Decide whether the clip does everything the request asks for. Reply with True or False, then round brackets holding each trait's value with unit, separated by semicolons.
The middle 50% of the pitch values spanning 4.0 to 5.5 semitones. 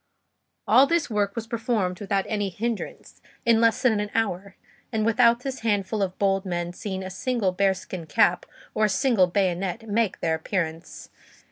False (3.5 semitones)